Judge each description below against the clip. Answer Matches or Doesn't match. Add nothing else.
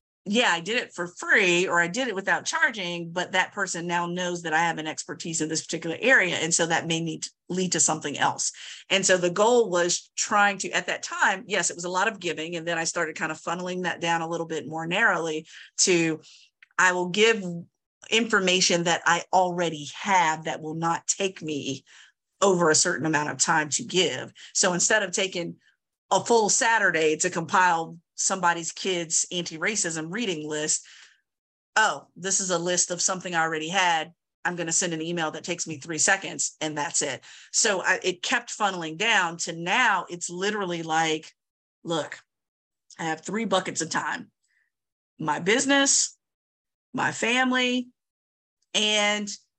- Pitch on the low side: Doesn't match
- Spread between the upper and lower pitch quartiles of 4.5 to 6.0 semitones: Doesn't match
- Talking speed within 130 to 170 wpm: Doesn't match